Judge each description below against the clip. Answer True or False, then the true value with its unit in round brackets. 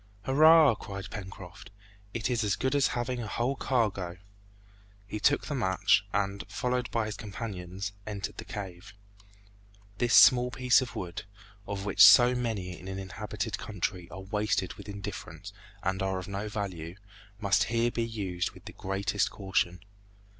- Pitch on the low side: True (105 Hz)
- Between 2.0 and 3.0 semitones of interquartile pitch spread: False (3.7 semitones)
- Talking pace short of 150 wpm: False (160 wpm)